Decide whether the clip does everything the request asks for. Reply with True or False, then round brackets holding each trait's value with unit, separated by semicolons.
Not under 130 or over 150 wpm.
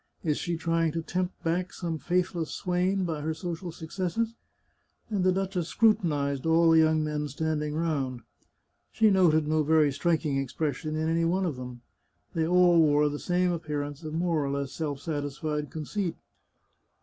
False (175 wpm)